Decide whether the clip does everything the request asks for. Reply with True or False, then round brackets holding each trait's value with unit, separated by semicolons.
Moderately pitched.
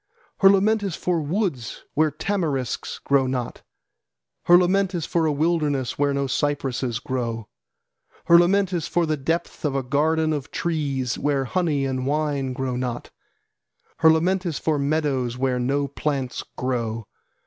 True (145 Hz)